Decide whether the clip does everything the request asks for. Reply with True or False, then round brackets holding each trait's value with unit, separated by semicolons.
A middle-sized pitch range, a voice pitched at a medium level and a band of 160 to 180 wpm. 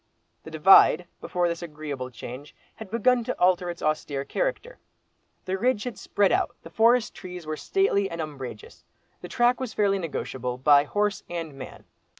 False (6.6 semitones; 180 Hz; 165 wpm)